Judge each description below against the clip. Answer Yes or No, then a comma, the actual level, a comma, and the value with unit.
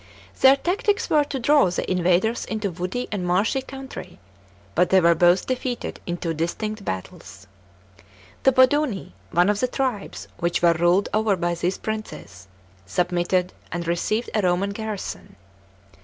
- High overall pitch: Yes, high, 195 Hz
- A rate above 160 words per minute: No, average, 150 wpm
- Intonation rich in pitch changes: Yes, wide, 5.8 semitones